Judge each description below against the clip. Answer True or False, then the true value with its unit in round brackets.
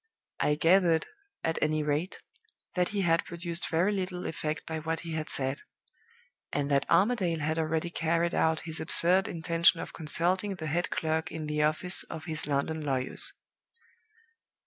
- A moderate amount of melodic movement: False (2.1 semitones)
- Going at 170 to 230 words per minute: False (160 wpm)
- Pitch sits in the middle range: True (165 Hz)